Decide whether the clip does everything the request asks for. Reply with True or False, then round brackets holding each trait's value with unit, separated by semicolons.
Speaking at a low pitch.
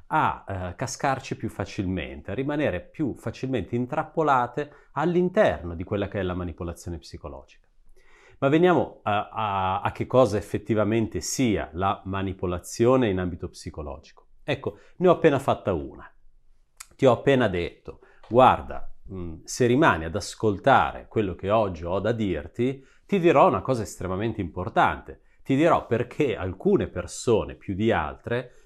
True (105 Hz)